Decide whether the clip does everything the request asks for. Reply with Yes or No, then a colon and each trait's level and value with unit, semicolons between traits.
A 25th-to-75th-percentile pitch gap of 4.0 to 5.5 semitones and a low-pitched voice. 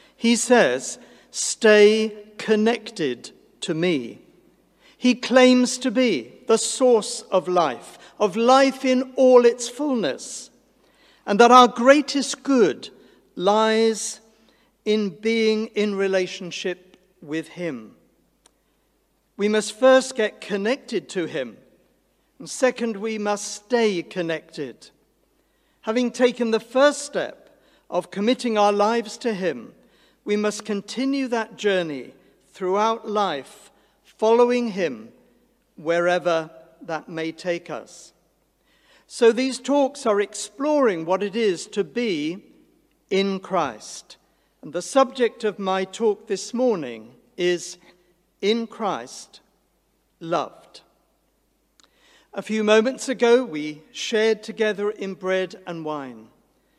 No: average, 4.4 semitones; high, 215 Hz